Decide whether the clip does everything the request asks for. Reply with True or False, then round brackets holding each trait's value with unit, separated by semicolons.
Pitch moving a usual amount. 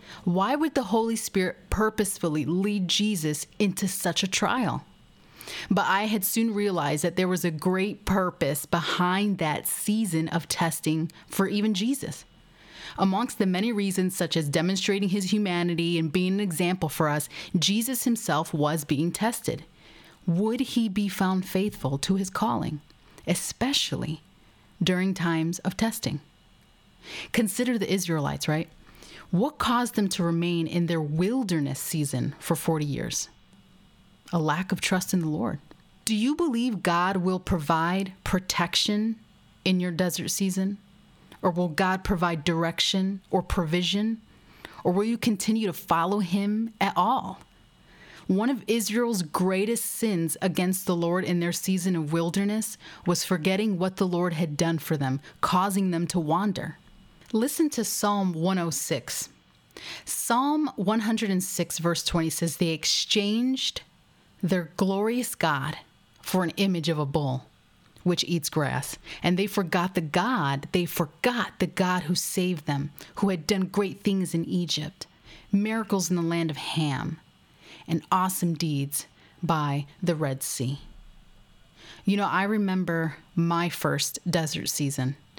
True (3.5 semitones)